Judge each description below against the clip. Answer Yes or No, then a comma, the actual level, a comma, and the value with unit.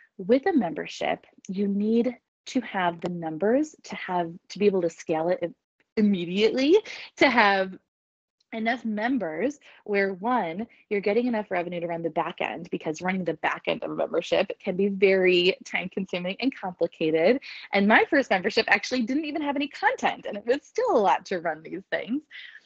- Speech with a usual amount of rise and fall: No, wide, 5.7 semitones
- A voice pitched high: Yes, high, 210 Hz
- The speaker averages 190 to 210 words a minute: No, average, 180 wpm